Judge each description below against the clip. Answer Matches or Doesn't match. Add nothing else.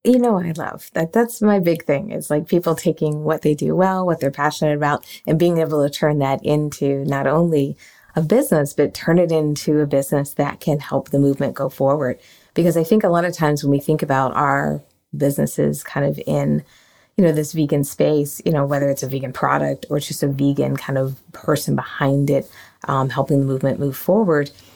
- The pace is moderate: Doesn't match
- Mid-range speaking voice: Matches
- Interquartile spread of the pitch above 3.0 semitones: Doesn't match